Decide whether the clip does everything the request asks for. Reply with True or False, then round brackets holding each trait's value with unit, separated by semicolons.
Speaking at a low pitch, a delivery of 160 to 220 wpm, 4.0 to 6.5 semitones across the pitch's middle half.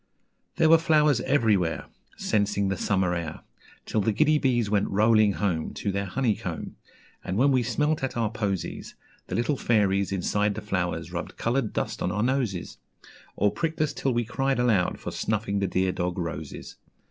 True (105 Hz; 175 wpm; 4.8 semitones)